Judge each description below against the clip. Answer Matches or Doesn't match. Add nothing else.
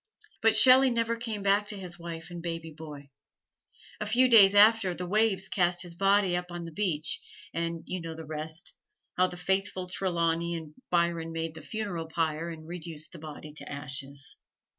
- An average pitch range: Matches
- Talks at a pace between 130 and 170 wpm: Doesn't match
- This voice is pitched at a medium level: Matches